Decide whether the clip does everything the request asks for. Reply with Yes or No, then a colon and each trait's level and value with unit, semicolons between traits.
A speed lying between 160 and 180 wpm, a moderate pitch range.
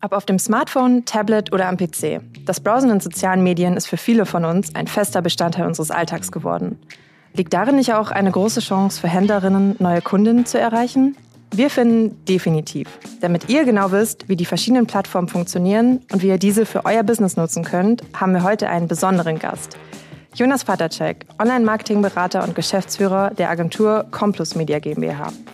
Yes: average, 175 wpm; average, 3.7 semitones